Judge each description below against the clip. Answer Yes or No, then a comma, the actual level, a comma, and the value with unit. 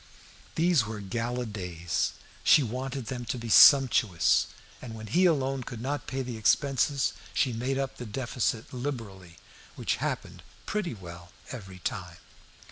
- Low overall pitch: Yes, low, 120 Hz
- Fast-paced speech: No, average, 150 wpm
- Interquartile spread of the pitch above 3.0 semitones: Yes, average, 4.5 semitones